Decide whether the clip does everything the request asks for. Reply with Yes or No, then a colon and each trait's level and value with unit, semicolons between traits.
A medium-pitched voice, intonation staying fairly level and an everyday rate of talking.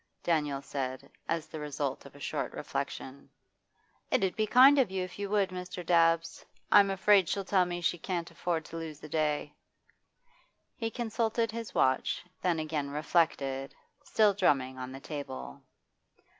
No: medium, 165 Hz; average, 5.1 semitones; average, 160 wpm